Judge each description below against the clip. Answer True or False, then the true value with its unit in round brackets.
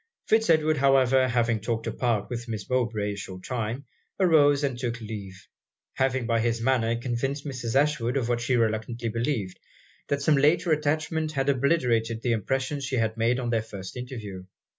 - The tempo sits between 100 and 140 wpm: False (175 wpm)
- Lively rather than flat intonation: False (3.4 semitones)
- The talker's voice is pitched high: False (120 Hz)